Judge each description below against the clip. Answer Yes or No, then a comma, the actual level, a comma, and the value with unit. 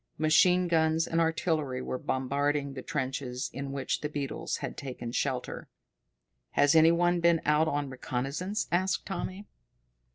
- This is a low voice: No, medium, 150 Hz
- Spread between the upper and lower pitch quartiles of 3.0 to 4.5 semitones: Yes, average, 3.6 semitones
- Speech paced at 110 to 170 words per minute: Yes, average, 140 wpm